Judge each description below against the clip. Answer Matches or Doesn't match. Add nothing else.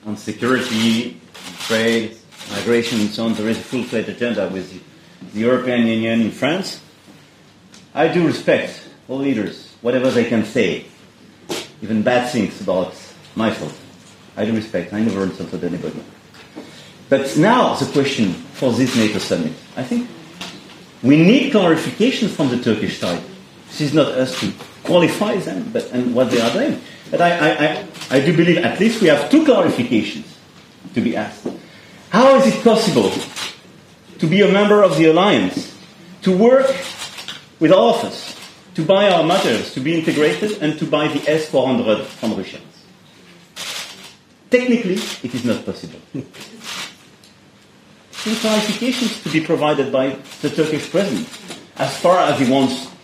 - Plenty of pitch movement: Matches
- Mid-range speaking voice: Matches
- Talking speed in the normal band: Matches